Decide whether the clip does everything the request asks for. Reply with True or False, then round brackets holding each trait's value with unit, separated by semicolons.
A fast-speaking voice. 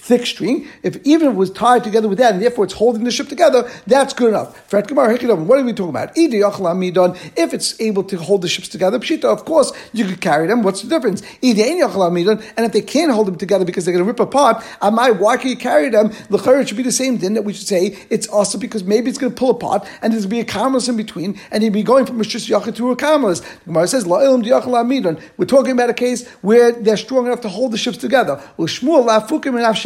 True (240 wpm)